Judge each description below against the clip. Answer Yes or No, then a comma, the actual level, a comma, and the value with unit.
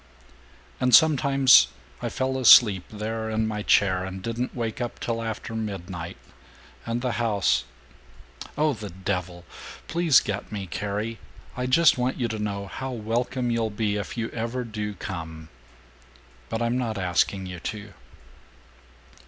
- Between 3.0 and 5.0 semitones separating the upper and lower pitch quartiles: Yes, average, 3.6 semitones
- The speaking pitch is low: Yes, low, 110 Hz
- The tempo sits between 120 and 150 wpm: Yes, average, 145 wpm